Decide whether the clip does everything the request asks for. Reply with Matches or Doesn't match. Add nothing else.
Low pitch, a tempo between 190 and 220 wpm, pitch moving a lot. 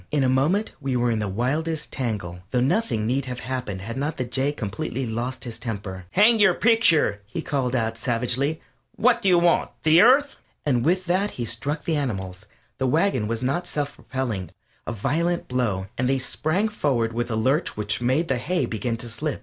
Matches